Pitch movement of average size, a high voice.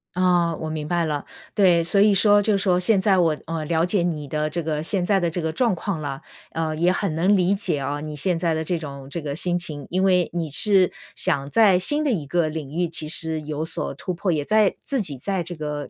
No: average, 3.4 semitones; medium, 170 Hz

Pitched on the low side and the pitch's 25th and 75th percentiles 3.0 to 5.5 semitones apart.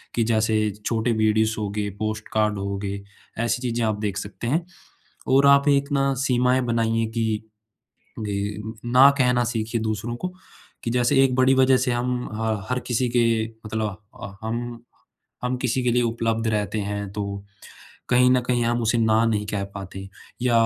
No: low, 115 Hz; narrow, 2.5 semitones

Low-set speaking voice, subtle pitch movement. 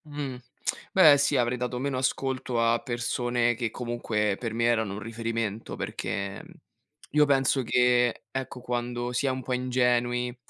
Yes: low, 120 Hz; narrow, 1.6 semitones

